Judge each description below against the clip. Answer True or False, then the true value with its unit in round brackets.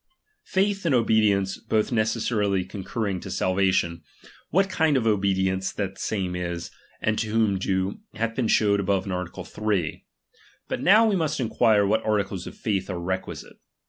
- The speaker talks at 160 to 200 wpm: True (165 wpm)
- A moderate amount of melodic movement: True (3.1 semitones)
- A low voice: True (100 Hz)